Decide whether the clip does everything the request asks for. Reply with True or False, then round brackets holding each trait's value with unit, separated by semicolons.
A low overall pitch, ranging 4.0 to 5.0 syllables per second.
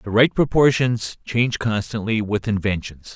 True (110 Hz; 4.6 syllables/s)